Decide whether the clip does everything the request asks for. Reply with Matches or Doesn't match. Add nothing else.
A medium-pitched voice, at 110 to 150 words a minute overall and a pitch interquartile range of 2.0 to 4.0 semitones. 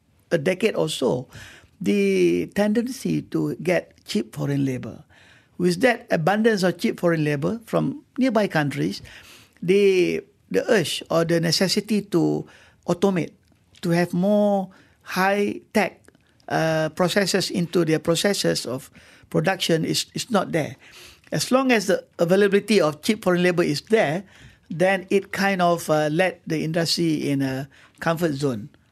Doesn't match